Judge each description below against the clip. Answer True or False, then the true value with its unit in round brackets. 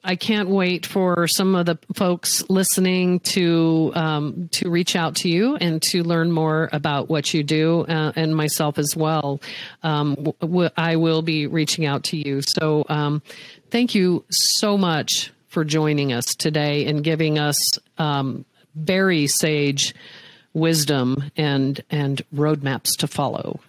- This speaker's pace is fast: False (150 wpm)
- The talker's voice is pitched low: False (160 Hz)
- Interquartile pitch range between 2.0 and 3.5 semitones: True (2.7 semitones)